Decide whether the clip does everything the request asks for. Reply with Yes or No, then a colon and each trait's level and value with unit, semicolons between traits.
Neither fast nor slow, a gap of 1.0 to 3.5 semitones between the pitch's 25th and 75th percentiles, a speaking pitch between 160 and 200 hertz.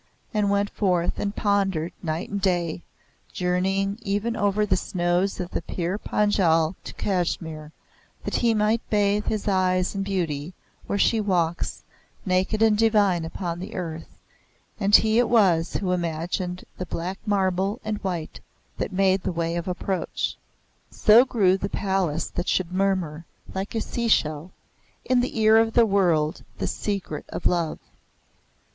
Yes: average, 150 wpm; average, 2.9 semitones; high, 190 Hz